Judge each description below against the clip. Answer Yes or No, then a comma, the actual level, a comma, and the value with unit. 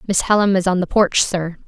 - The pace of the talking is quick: Yes, fast, 250 wpm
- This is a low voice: No, high, 190 Hz